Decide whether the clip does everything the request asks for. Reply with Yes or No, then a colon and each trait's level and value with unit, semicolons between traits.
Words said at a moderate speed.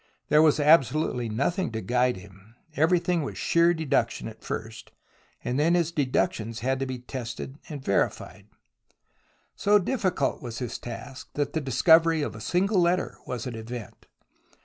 Yes: average, 155 wpm